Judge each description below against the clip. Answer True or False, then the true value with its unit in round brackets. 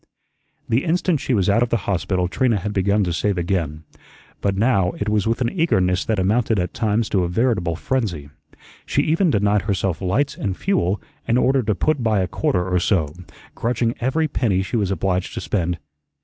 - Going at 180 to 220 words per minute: True (195 wpm)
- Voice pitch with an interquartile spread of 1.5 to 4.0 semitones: False (4.4 semitones)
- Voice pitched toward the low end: True (100 Hz)